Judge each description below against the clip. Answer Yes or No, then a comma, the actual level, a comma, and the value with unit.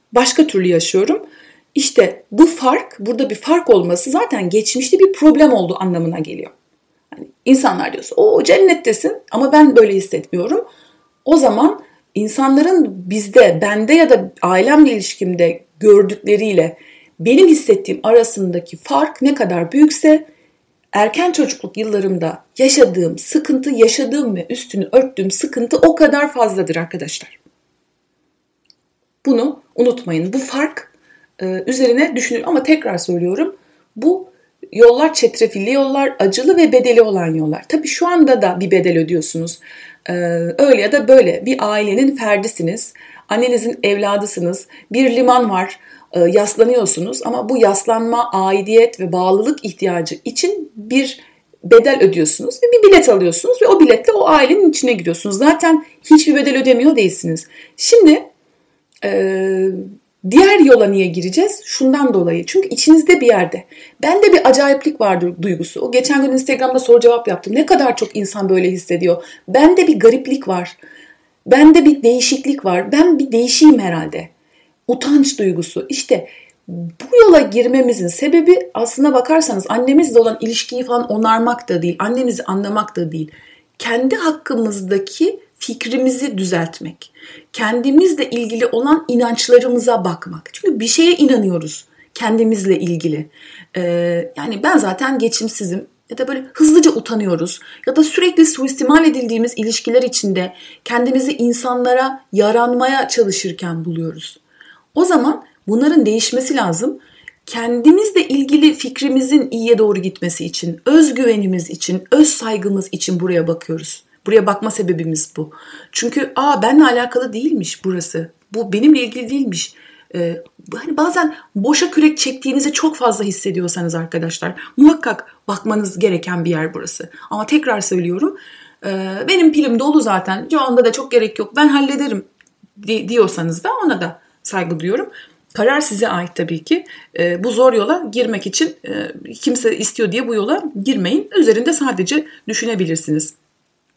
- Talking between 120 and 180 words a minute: Yes, average, 130 wpm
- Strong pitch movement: Yes, wide, 7.6 semitones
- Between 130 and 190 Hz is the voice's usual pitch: No, high, 240 Hz